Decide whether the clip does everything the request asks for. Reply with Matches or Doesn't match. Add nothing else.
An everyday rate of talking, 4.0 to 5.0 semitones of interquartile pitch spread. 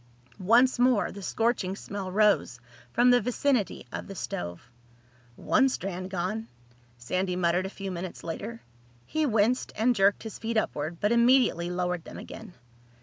Matches